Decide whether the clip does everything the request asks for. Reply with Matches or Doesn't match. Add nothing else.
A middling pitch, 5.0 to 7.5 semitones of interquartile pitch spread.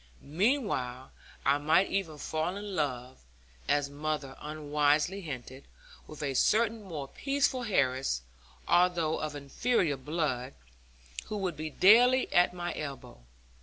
Matches